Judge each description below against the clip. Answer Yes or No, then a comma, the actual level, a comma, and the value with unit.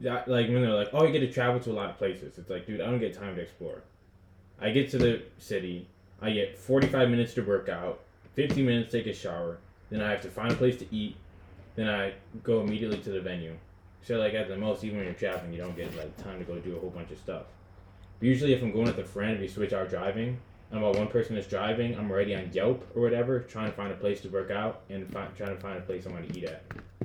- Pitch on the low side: Yes, low, 105 Hz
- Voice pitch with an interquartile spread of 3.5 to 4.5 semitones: Yes, average, 3.8 semitones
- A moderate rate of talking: No, fast, 275 wpm